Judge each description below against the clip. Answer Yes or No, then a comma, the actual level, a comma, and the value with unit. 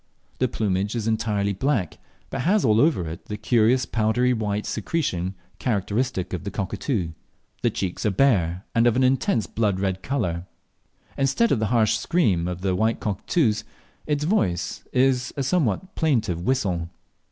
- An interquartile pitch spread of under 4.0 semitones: No, average, 5.3 semitones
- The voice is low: Yes, low, 110 Hz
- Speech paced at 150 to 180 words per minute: Yes, average, 155 wpm